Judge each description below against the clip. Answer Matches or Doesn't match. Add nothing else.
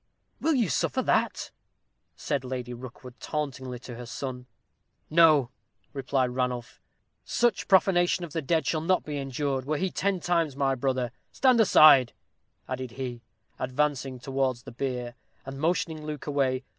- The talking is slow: Doesn't match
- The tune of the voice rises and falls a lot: Doesn't match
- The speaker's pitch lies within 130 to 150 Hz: Matches